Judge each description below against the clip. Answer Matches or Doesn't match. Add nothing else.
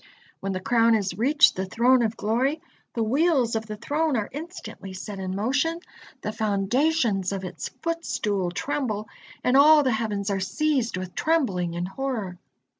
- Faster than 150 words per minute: Matches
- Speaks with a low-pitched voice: Doesn't match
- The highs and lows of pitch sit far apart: Matches